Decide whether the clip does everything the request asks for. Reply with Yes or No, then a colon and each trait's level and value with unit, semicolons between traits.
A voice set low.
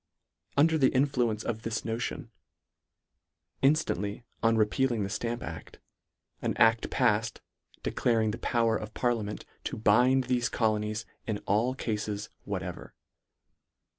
Yes: low, 115 Hz